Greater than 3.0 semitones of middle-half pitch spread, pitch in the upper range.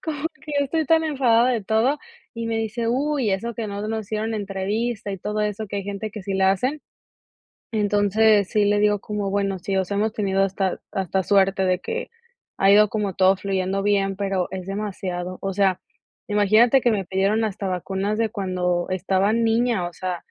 No: narrow, 2.6 semitones; high, 205 Hz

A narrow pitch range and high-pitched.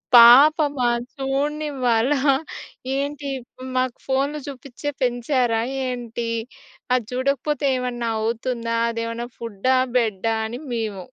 No: average, 3.1 semitones; very high, 250 Hz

